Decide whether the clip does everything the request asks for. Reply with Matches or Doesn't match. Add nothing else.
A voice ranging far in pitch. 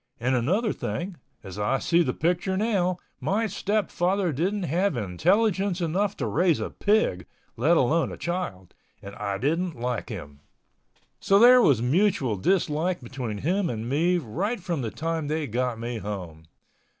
Matches